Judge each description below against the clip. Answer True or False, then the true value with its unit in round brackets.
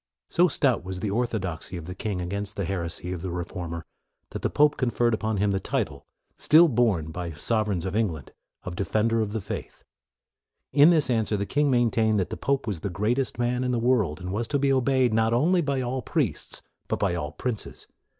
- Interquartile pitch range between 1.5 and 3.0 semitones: False (5.3 semitones)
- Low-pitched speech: True (110 Hz)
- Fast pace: True (215 wpm)